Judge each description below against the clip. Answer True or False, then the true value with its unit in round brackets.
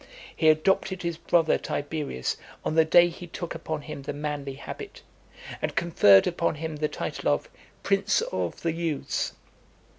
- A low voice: False (160 Hz)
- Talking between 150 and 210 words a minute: True (155 wpm)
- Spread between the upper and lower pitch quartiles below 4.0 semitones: True (2.5 semitones)